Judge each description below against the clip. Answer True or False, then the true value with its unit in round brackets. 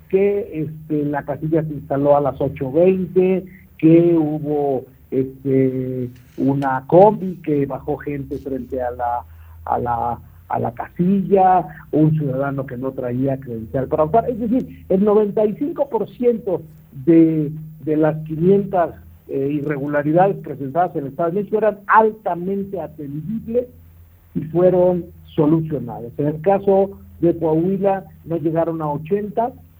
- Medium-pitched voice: True (155 Hz)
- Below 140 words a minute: True (125 wpm)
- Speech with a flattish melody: False (5.4 semitones)